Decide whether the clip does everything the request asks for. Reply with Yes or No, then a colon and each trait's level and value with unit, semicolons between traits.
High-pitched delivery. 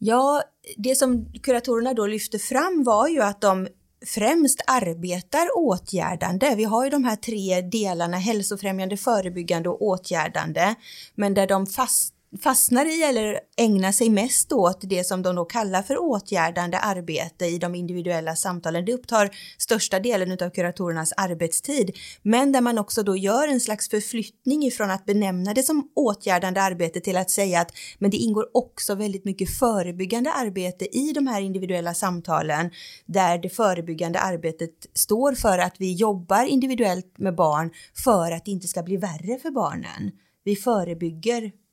Yes: high, 200 Hz